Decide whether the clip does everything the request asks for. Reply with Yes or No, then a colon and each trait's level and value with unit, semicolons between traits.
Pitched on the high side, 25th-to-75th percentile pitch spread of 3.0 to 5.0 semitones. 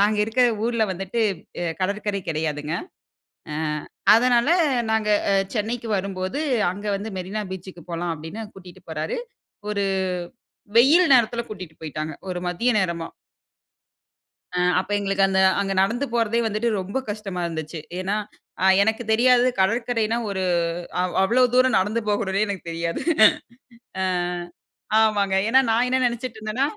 Yes: high, 205 Hz; average, 3.9 semitones